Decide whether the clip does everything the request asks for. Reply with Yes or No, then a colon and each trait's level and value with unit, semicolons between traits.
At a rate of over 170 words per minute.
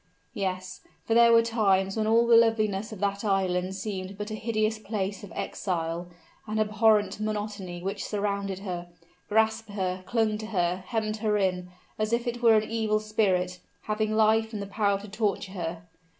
Yes: average, 180 wpm